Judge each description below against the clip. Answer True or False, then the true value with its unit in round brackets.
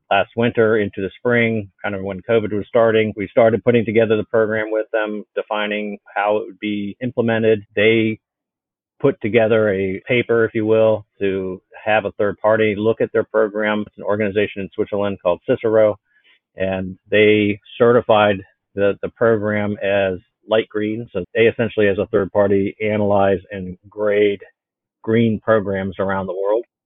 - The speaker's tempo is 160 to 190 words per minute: True (165 wpm)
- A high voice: False (105 Hz)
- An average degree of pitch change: False (1.8 semitones)